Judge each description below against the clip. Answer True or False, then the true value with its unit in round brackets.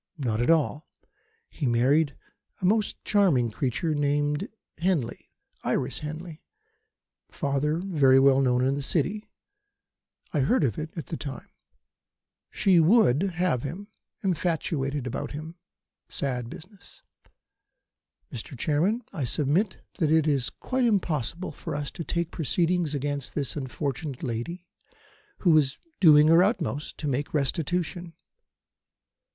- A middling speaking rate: False (125 wpm)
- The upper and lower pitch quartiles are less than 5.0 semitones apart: True (4.1 semitones)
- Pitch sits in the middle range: True (150 Hz)